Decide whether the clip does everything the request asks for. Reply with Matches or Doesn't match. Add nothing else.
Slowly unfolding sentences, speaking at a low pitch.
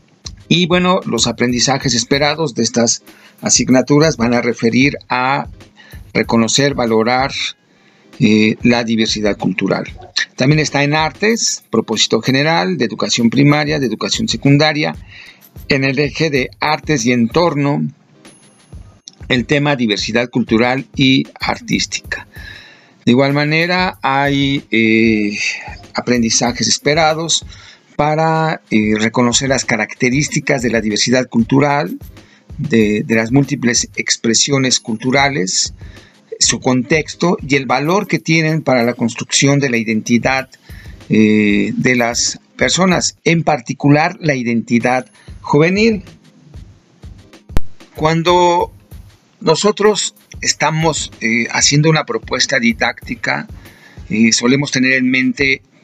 Matches